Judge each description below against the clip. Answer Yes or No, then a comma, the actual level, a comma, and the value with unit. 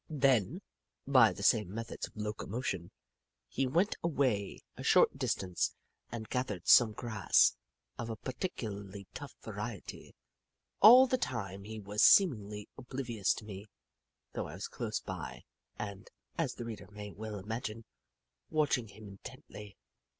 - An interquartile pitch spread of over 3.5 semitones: Yes, average, 4.1 semitones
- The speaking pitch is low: Yes, low, 110 Hz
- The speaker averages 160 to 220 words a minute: No, slow, 135 wpm